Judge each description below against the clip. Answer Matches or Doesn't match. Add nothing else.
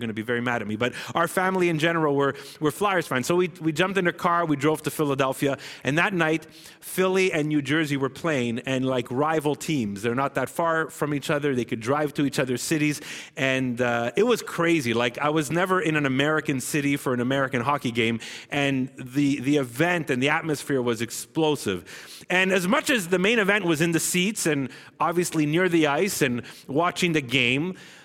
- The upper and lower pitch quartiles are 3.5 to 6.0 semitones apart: Matches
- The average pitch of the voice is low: Doesn't match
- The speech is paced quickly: Matches